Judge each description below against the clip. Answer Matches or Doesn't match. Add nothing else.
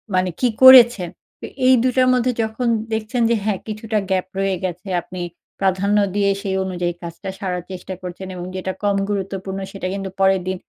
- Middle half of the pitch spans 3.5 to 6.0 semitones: Doesn't match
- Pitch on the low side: Doesn't match